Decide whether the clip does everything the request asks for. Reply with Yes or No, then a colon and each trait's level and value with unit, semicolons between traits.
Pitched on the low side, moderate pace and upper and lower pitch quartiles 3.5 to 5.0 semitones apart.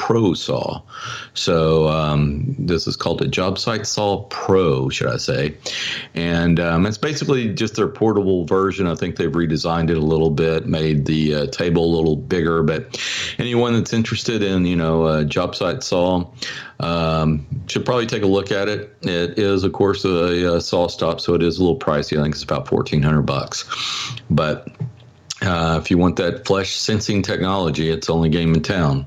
Yes: very low, 85 Hz; average, 185 wpm; average, 3.8 semitones